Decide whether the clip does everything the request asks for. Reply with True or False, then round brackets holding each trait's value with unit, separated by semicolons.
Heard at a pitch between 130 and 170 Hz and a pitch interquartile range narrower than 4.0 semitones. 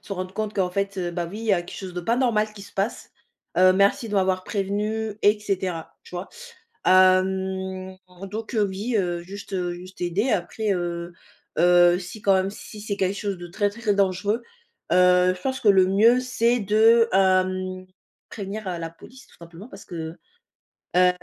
False (190 Hz; 2.5 semitones)